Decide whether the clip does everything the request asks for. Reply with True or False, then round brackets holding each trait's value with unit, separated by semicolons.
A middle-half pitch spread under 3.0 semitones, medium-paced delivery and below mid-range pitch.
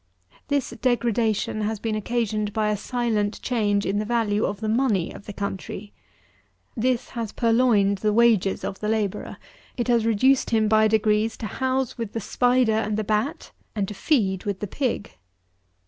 False (2.4 semitones; 175 wpm; 220 Hz)